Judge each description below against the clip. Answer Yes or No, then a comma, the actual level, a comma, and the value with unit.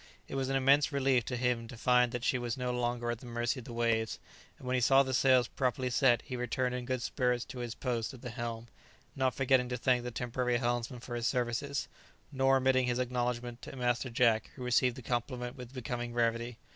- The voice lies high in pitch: No, low, 125 Hz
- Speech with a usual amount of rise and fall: No, narrow, 1.4 semitones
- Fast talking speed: Yes, fast, 225 wpm